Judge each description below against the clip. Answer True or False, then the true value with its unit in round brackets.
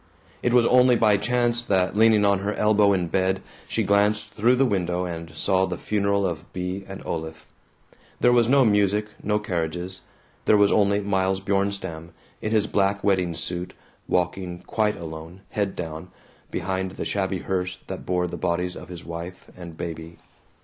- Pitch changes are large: False (2.8 semitones)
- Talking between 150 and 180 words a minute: True (170 wpm)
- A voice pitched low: True (95 Hz)